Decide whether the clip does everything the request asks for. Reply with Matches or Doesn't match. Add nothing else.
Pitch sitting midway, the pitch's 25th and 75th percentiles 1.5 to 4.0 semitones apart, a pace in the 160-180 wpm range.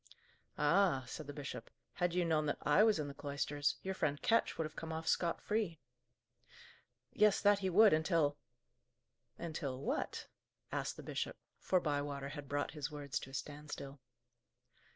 Matches